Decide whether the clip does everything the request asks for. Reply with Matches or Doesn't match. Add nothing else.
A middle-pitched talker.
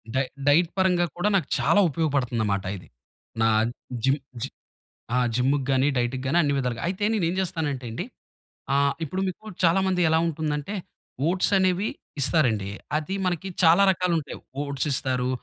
Matches